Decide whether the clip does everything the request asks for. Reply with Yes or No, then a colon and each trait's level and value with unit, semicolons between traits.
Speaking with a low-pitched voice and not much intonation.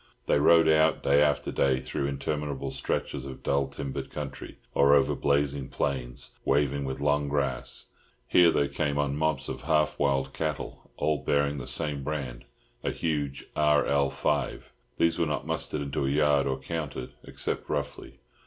Yes: very low, 70 Hz; narrow, 1.5 semitones